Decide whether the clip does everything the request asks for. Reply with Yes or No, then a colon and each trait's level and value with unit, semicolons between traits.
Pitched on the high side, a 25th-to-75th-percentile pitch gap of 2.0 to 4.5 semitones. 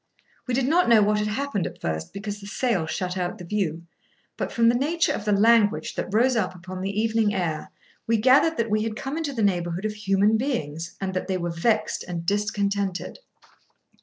Yes: high, 210 Hz; average, 3.9 semitones